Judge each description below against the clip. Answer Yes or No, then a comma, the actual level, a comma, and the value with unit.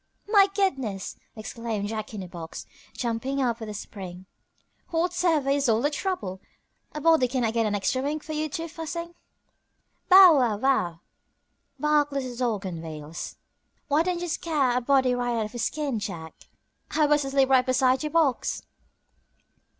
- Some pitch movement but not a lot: No, wide, 5.7 semitones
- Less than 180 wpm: Yes, average, 165 wpm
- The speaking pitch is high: Yes, very high, 260 Hz